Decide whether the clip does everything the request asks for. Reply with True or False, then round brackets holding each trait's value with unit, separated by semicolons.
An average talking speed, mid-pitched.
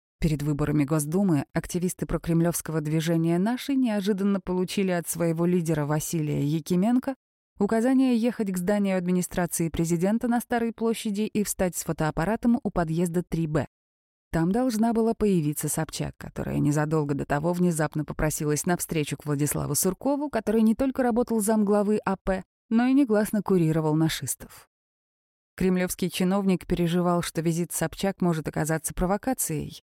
True (130 wpm; 180 Hz)